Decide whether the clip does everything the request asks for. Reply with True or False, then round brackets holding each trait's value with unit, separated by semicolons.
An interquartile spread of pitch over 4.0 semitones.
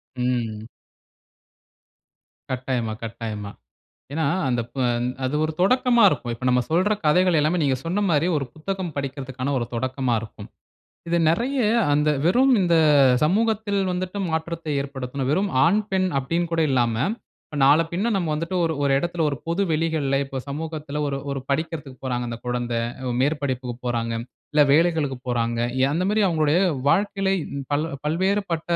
True (5.2 semitones)